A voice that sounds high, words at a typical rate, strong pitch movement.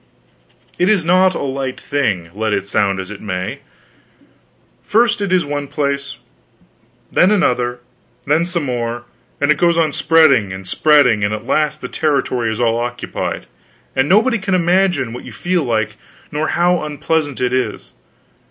No: medium, 140 Hz; average, 160 wpm; wide, 6.5 semitones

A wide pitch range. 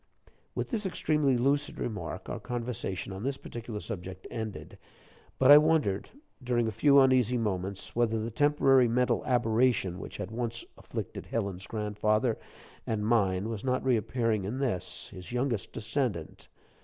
No: average, 3.7 semitones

